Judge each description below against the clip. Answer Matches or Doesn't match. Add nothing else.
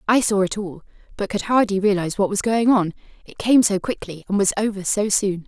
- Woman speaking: Matches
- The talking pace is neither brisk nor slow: Doesn't match